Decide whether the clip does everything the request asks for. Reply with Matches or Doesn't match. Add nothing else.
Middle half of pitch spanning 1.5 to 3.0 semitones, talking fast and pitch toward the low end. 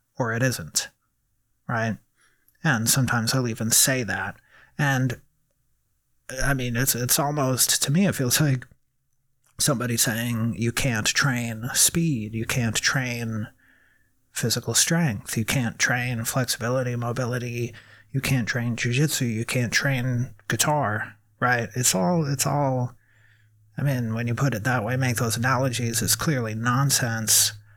Doesn't match